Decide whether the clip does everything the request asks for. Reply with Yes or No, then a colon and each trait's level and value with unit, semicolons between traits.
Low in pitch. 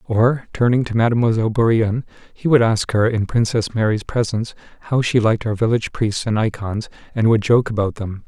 Yes: low, 110 Hz